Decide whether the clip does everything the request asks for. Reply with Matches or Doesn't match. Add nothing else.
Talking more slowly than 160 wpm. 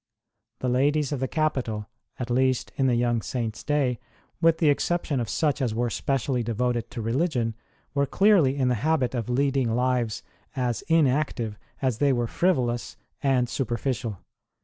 Doesn't match